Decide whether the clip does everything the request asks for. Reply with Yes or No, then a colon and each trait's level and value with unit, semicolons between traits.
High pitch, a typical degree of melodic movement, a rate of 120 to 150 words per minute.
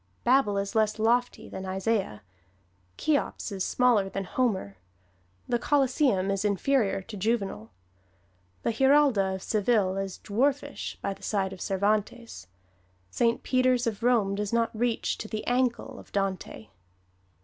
Yes: high, 215 Hz; average, 3.9 semitones; average, 140 wpm